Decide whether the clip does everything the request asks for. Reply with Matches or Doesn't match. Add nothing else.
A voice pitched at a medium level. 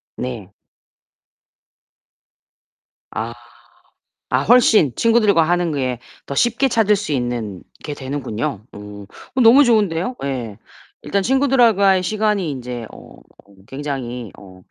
Matches